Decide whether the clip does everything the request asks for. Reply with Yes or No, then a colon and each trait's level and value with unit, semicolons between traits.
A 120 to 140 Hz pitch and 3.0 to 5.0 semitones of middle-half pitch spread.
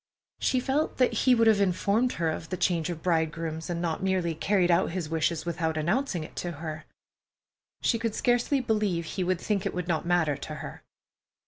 No: medium, 175 Hz; average, 4.5 semitones